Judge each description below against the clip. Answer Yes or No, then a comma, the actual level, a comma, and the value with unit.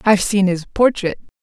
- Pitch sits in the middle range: No, high, 200 Hz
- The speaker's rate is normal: Yes, average, 170 wpm